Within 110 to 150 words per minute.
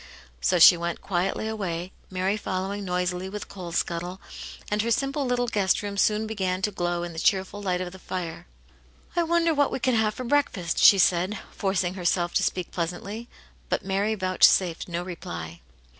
No: average, 185 wpm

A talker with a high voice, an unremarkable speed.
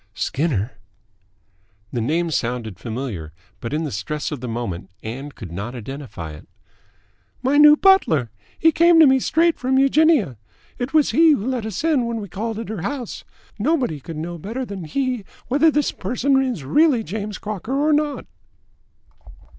Yes: high, 210 Hz; average, 170 wpm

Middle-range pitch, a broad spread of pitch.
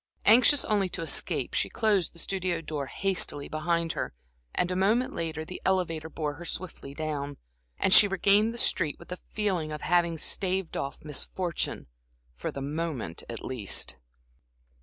No: medium, 170 Hz; average, 3.7 semitones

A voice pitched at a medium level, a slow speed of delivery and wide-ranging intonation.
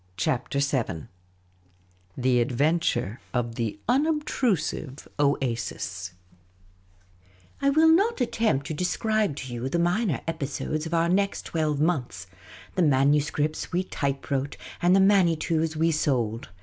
Yes: medium, 150 Hz; slow, 125 wpm; wide, 5.7 semitones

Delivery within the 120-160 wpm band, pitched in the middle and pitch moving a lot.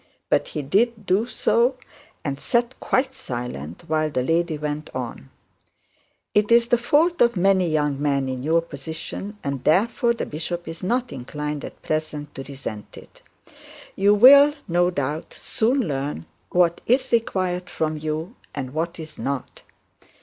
Yes: average, 155 wpm; medium, 165 Hz; wide, 7.7 semitones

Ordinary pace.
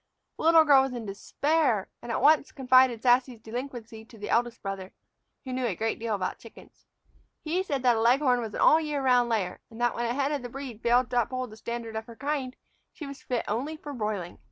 No: fast, 230 wpm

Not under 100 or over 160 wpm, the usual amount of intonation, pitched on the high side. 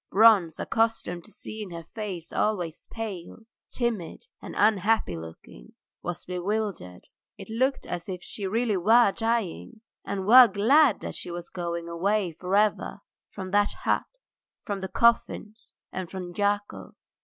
Yes: average, 145 wpm; average, 4.0 semitones; high, 200 Hz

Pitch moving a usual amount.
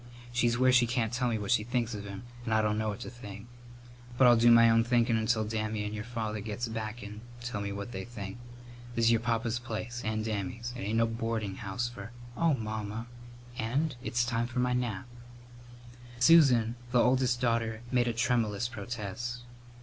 No: narrow, 2.0 semitones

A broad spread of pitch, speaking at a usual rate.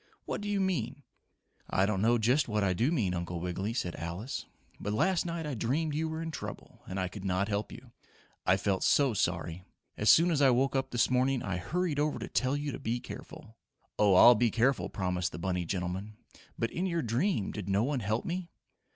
No: wide, 7.1 semitones; fast, 220 wpm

